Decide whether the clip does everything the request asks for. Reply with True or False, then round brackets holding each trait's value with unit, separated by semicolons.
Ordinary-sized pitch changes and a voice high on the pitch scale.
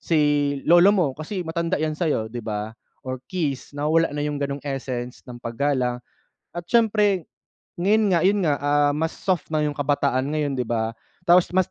False (4.7 semitones; 150 Hz)